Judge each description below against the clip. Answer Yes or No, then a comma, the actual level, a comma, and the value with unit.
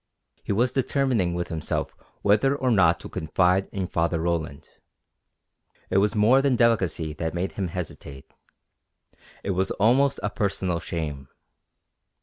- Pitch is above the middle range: No, very low, 95 Hz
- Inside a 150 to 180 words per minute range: No, slow, 135 wpm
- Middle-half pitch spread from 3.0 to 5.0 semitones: No, wide, 5.5 semitones